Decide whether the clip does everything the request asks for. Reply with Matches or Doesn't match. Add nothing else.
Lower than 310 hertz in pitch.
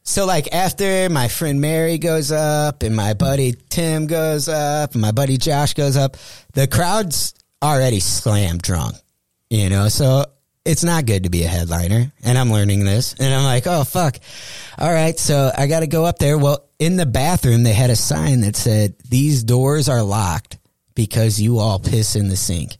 Matches